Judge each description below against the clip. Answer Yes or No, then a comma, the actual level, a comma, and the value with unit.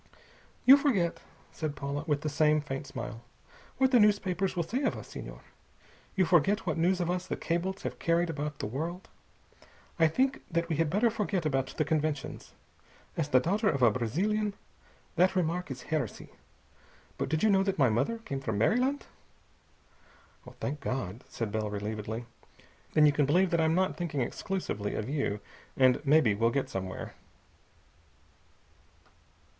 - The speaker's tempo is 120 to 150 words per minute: No, average, 165 wpm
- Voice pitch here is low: No, medium, 155 Hz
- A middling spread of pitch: No, wide, 5.8 semitones